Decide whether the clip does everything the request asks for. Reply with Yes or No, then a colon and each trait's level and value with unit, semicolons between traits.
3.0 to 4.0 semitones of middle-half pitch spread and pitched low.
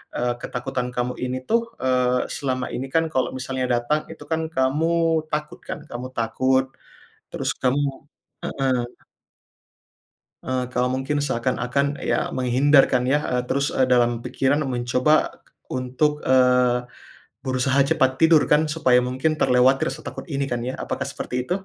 No: narrow, 2.4 semitones; low, 130 Hz